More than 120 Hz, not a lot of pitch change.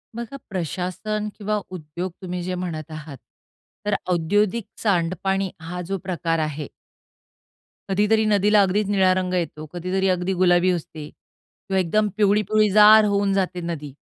No: medium, 185 Hz; average, 3.0 semitones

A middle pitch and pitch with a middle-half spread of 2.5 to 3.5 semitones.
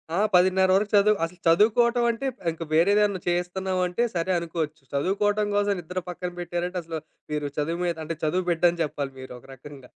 Yes: medium, 175 Hz; average, 3.2 semitones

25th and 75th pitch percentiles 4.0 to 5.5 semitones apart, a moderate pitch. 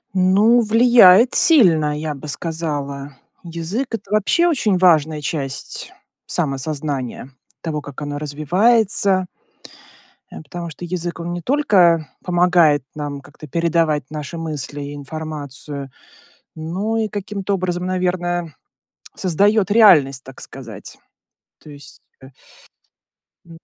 Yes: average, 4.3 semitones; medium, 165 Hz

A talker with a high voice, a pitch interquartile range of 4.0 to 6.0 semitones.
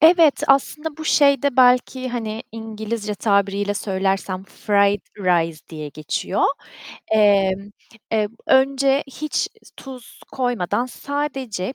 Yes: high, 220 Hz; average, 5.3 semitones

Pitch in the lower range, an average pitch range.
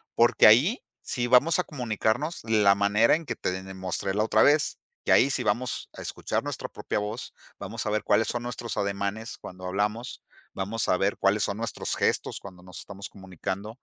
Yes: low, 110 Hz; average, 3.4 semitones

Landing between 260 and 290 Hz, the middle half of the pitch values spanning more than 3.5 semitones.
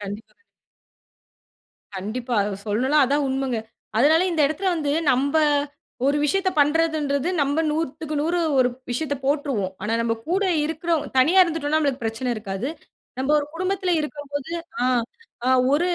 Yes: very high, 285 Hz; average, 3.9 semitones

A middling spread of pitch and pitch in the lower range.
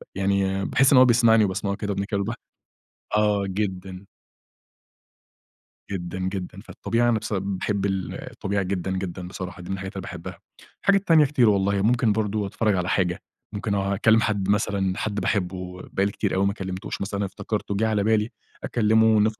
No: narrow, 2.2 semitones; low, 100 Hz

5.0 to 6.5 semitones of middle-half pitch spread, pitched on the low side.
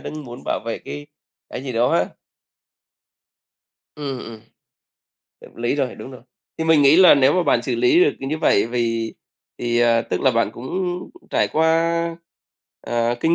Yes: average, 5.3 semitones; low, 130 Hz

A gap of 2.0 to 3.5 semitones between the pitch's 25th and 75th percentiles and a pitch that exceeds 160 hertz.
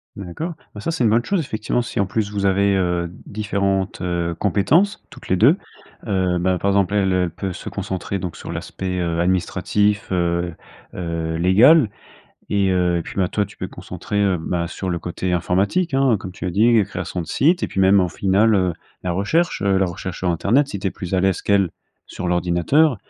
No: average, 2.8 semitones; very low, 95 Hz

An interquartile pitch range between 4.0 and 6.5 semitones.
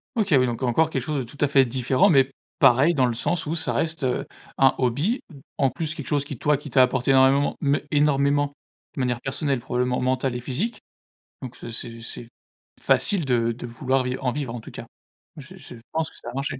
No: average, 2.9 semitones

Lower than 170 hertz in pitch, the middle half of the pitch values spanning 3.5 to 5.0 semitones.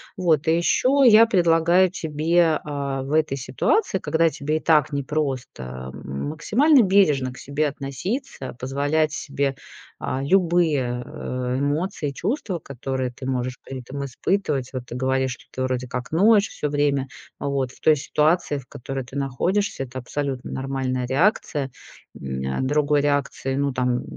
Yes: medium, 140 Hz; average, 3.8 semitones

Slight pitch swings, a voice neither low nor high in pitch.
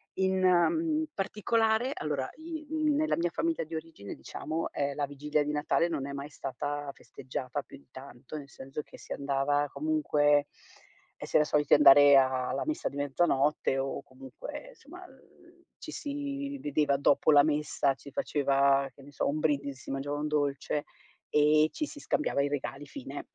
No: average, 5.2 semitones; medium, 145 Hz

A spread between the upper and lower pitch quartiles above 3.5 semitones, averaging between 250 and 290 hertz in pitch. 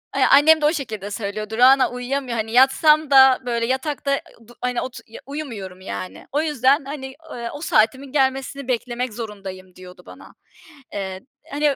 Yes: average, 4.0 semitones; very high, 255 Hz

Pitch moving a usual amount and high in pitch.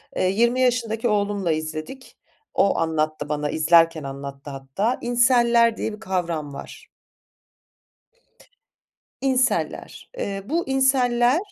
No: wide, 7.6 semitones; high, 205 Hz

